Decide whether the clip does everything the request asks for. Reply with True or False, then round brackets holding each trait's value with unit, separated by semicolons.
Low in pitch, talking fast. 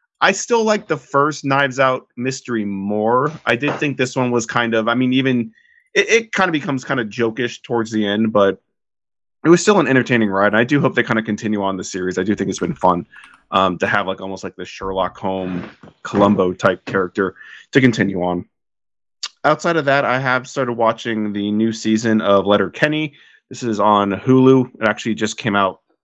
True (115 Hz; 210 wpm)